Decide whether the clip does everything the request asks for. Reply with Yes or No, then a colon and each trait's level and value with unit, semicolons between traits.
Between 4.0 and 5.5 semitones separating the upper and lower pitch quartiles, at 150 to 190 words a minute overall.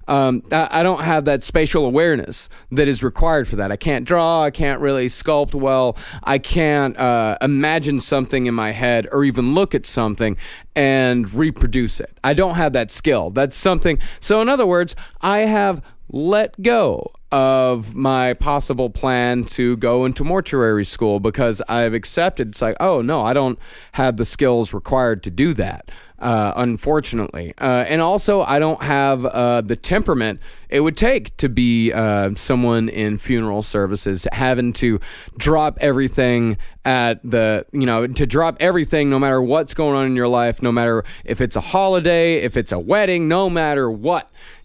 Yes: average, 4.5 semitones; average, 175 wpm